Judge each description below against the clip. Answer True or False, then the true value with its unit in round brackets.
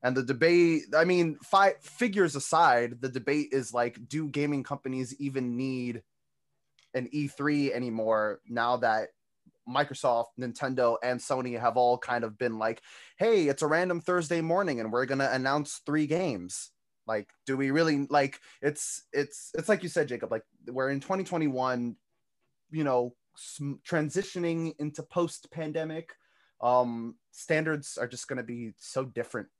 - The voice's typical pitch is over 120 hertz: True (135 Hz)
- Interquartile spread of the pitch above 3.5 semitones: True (4.3 semitones)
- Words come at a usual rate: True (155 wpm)